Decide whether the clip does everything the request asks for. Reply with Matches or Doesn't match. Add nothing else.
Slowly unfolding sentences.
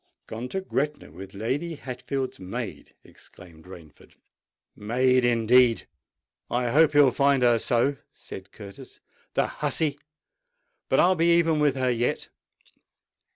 Matches